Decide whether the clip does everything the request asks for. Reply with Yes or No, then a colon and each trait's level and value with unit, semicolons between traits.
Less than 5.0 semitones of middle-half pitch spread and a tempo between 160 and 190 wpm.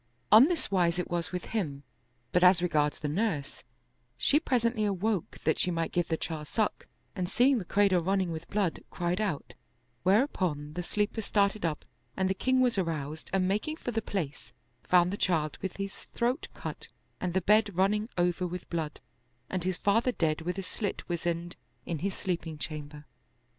Yes: average, 3.8 semitones; average, 185 wpm